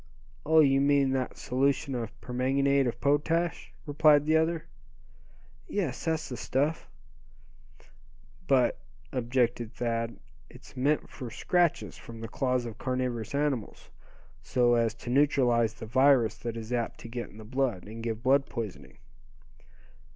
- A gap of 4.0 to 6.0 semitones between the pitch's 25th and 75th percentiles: No, average, 3.3 semitones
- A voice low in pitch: Yes, low, 125 Hz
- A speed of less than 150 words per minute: Yes, average, 140 wpm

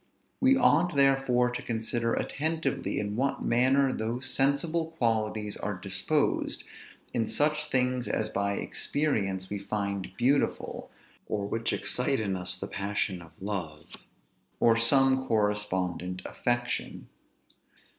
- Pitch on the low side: Yes, low, 115 Hz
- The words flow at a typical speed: No, slow, 120 wpm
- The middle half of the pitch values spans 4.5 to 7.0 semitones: Yes, average, 5.1 semitones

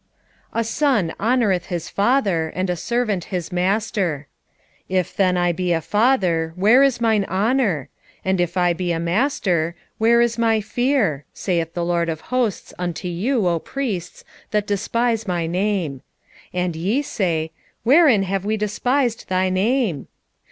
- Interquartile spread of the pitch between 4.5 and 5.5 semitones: Yes, average, 4.9 semitones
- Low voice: No, high, 190 Hz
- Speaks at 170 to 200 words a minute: No, average, 155 wpm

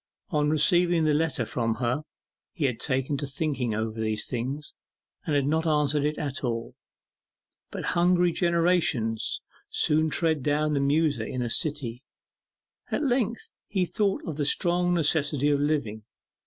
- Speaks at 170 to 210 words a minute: No, average, 155 wpm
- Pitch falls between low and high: Yes, medium, 150 Hz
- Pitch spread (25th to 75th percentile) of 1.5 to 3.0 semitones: No, average, 4.2 semitones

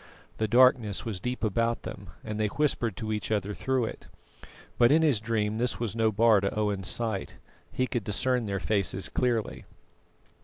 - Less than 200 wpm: Yes, average, 180 wpm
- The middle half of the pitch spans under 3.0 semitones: Yes, narrow, 2.6 semitones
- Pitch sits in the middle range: No, low, 110 Hz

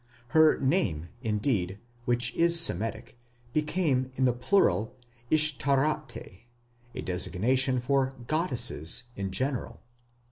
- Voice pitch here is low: Yes, low, 130 Hz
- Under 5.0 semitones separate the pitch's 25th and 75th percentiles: No, wide, 5.4 semitones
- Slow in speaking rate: Yes, slow, 100 wpm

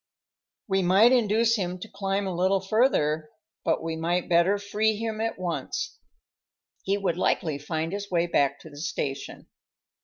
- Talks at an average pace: Yes, average, 160 wpm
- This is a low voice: No, medium, 185 Hz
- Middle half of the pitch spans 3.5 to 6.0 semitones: Yes, average, 3.9 semitones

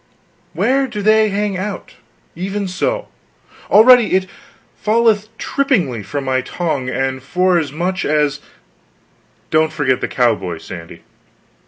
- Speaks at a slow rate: Yes, slow, 120 wpm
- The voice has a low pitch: No, medium, 180 Hz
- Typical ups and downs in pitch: No, wide, 7.8 semitones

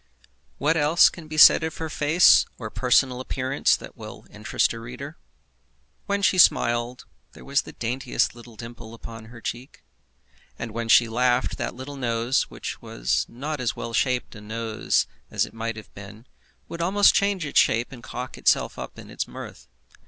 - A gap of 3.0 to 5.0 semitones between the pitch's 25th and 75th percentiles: Yes, average, 4.1 semitones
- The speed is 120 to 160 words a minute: No, average, 180 wpm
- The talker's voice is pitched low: Yes, low, 125 Hz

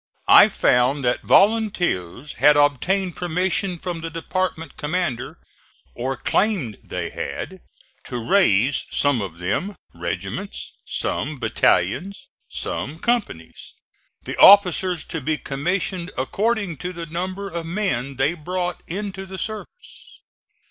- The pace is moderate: No, slow, 120 wpm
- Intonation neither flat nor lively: No, wide, 6.3 semitones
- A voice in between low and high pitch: Yes, medium, 170 Hz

